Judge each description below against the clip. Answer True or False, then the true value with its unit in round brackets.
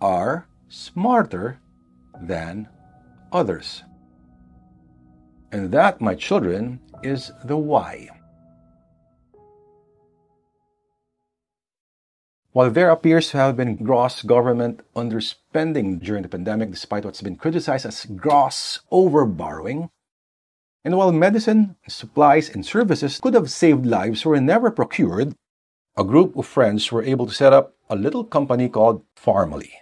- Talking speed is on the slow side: True (115 wpm)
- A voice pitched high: False (115 Hz)